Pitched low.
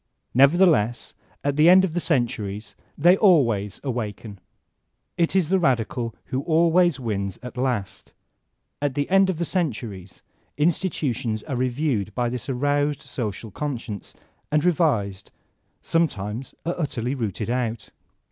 Yes: low, 130 Hz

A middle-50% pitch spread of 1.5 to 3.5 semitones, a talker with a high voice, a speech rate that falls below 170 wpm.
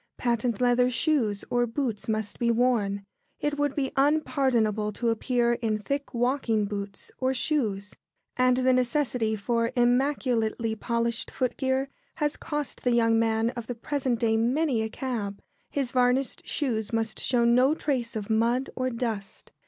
Yes: average, 2.7 semitones; high, 240 Hz; average, 155 wpm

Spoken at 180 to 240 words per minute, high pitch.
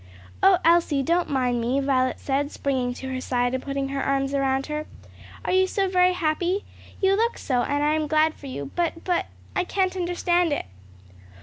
Yes: average, 195 wpm; very high, 295 Hz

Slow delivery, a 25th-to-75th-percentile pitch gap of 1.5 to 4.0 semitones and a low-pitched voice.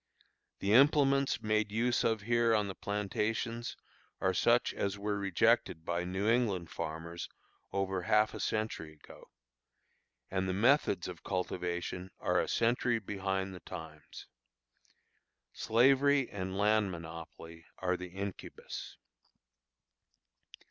Yes: slow, 120 wpm; average, 3.7 semitones; low, 100 Hz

